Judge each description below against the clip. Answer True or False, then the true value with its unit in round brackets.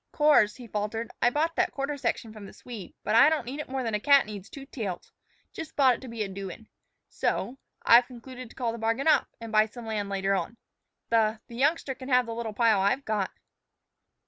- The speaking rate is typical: False (225 wpm)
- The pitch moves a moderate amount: True (3.8 semitones)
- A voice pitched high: True (230 Hz)